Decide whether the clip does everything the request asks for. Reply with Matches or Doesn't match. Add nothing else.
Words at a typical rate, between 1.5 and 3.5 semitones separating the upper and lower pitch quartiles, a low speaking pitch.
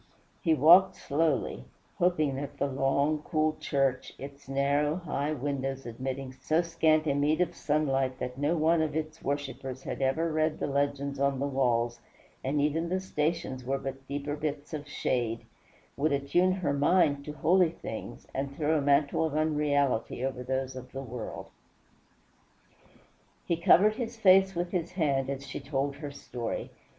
Doesn't match